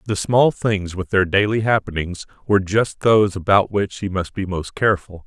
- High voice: No, low, 100 Hz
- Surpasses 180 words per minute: Yes, average, 195 wpm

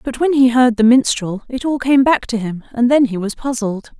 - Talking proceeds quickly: Yes, fast, 255 wpm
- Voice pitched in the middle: No, high, 245 Hz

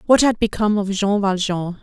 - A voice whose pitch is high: Yes, high, 205 Hz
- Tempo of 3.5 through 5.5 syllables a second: Yes, 5.4 syllables/s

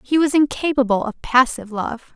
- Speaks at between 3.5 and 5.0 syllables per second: No, 5.4 syllables/s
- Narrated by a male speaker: No, female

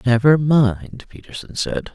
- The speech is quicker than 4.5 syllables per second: No, 3.9 syllables/s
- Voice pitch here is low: Yes, low, 130 Hz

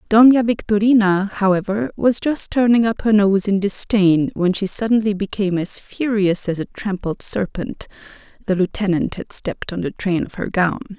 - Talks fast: No, average, 165 wpm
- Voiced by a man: No, female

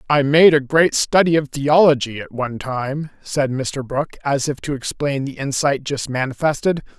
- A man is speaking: Yes, male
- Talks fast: No, average, 180 wpm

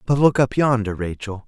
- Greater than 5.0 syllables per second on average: Yes, 5.3 syllables/s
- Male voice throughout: Yes, male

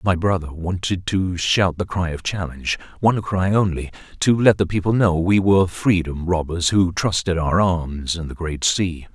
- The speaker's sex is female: No, male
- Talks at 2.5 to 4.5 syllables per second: No, 4.7 syllables/s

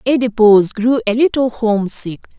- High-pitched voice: Yes, high, 235 Hz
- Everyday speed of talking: Yes, average, 150 wpm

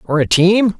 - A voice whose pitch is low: No, medium, 185 Hz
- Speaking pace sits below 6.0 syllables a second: Yes, 4.4 syllables/s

